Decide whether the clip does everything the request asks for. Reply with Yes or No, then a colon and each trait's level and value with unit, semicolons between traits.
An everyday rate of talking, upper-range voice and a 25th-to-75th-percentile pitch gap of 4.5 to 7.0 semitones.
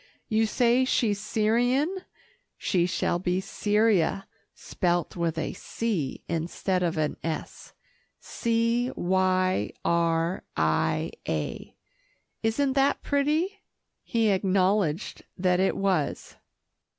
No: slow, 100 wpm; high, 195 Hz; average, 5.0 semitones